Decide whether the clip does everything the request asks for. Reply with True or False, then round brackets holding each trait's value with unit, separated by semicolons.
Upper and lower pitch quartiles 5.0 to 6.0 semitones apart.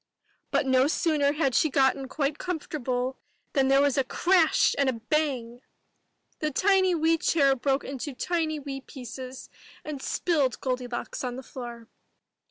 False (3.2 semitones)